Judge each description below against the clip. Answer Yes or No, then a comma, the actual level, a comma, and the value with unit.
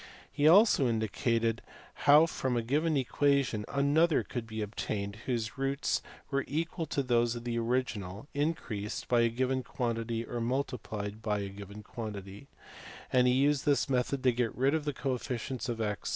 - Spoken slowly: No, average, 170 wpm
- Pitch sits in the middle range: No, low, 125 Hz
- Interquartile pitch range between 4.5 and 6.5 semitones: No, average, 3.8 semitones